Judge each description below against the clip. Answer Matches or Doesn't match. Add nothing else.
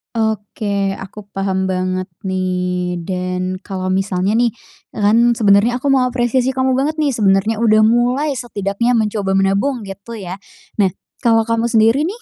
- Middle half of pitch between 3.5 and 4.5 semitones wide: Matches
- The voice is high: Matches